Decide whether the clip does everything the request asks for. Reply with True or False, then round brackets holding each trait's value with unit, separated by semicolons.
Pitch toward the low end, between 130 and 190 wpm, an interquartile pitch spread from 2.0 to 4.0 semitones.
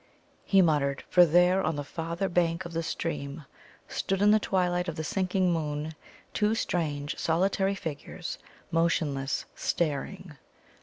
False (170 Hz; 140 wpm; 3.4 semitones)